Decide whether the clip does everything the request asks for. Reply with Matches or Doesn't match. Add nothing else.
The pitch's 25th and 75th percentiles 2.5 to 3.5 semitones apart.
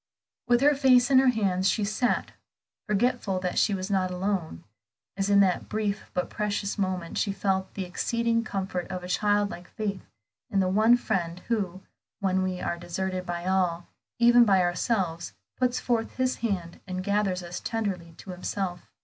Matches